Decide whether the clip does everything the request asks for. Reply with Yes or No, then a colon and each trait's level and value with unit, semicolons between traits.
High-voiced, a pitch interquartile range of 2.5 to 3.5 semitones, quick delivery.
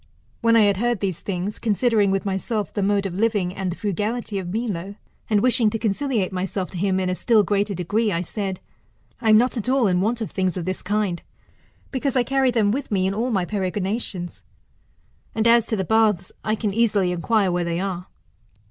Yes: high, 205 Hz; average, 3.2 semitones; fast, 210 wpm